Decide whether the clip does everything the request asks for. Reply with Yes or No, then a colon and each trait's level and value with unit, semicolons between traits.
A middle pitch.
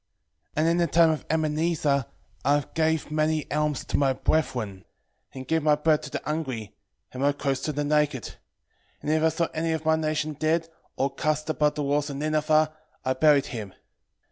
Yes: medium, 150 Hz